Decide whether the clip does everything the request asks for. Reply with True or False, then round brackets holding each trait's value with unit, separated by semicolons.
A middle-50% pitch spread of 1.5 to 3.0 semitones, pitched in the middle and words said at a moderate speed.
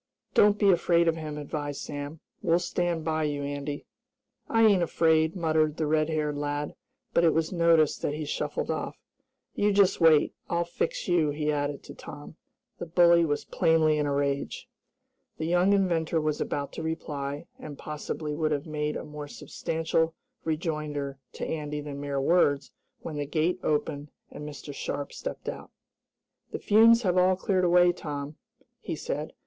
True (2.7 semitones; 155 Hz; 170 wpm)